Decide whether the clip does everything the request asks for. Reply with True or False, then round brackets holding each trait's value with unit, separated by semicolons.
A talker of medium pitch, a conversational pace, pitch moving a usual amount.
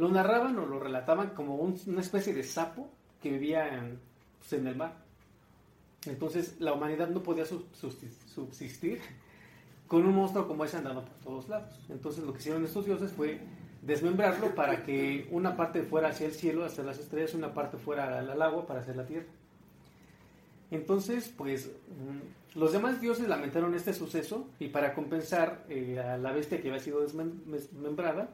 True (160 Hz; 170 wpm; 3.5 semitones)